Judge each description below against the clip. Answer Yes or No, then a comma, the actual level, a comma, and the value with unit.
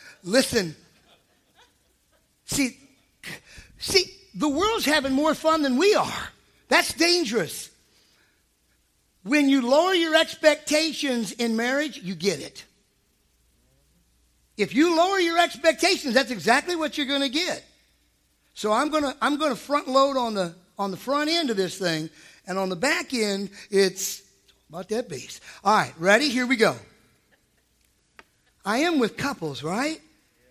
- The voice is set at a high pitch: Yes, very high, 250 Hz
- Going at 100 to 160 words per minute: Yes, average, 140 wpm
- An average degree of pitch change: No, wide, 8.5 semitones